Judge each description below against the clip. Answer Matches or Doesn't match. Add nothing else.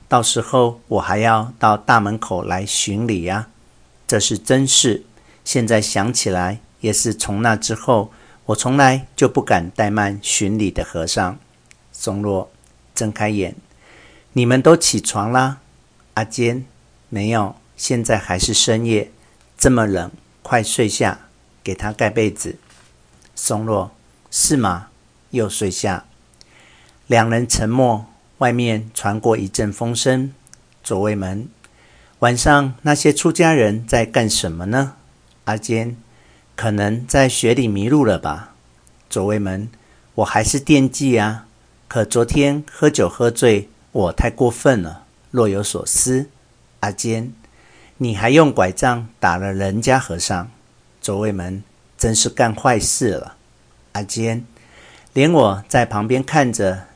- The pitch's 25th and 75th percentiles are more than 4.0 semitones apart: Doesn't match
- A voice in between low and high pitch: Doesn't match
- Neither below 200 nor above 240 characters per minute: Doesn't match